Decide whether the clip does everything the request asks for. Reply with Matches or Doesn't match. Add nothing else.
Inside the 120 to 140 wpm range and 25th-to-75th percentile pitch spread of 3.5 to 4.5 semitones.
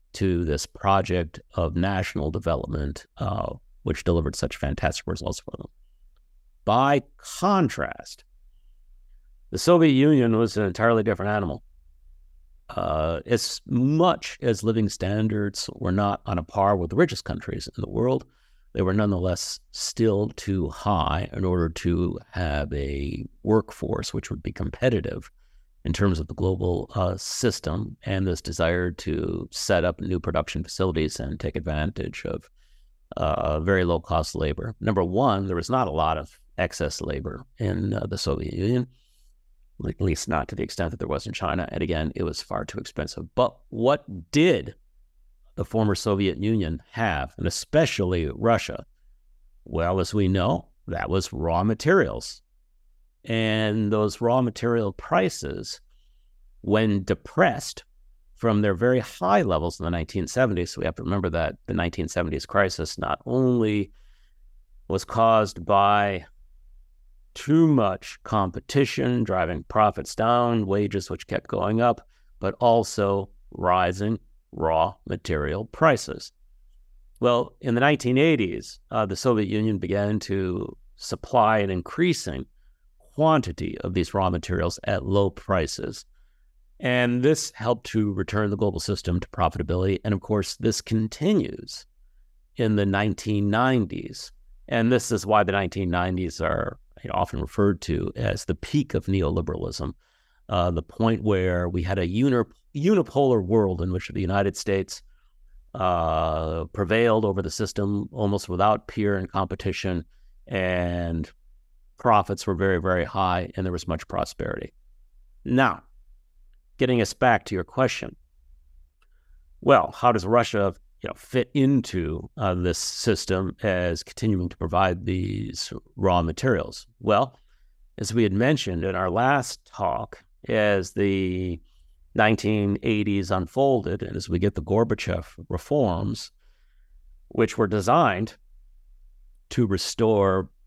Matches